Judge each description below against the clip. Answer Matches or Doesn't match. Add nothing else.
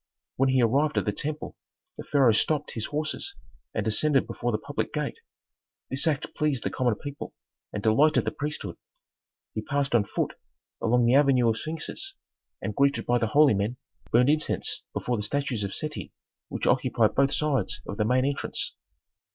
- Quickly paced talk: Doesn't match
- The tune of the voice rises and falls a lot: Doesn't match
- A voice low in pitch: Matches